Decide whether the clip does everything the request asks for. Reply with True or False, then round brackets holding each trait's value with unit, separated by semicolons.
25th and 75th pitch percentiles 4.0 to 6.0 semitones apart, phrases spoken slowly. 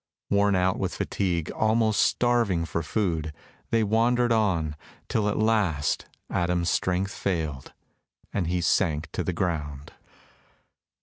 True (4.8 semitones; 125 wpm)